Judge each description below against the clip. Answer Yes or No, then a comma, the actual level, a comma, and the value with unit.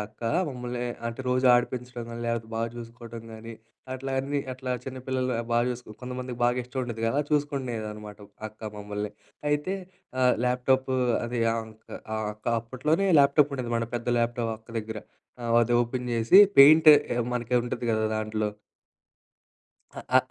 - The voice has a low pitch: Yes, low, 120 Hz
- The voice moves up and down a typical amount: No, narrow, 2.3 semitones